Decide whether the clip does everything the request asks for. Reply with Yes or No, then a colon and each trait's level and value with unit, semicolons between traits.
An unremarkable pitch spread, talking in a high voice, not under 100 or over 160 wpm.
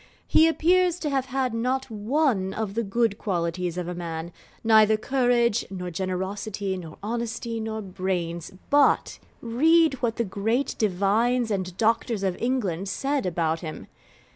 Yes: average, 4.8 semitones; high, 220 Hz; average, 145 wpm